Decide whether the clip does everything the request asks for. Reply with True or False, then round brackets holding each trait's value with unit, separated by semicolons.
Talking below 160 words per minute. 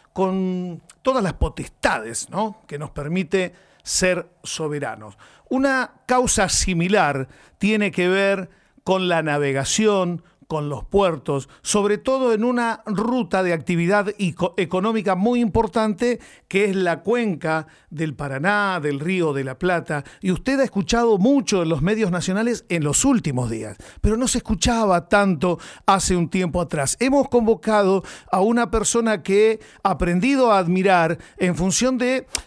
True (145 wpm)